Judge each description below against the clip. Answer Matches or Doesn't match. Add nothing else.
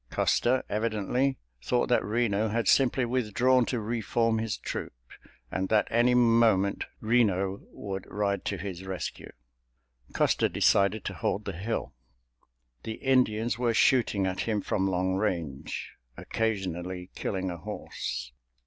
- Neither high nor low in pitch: Doesn't match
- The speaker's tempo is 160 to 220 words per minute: Doesn't match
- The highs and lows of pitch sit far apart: Doesn't match